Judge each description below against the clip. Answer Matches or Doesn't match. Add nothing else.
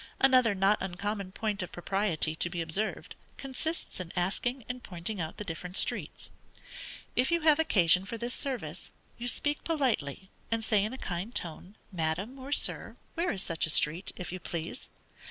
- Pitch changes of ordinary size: Doesn't match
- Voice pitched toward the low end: Doesn't match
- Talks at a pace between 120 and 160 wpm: Doesn't match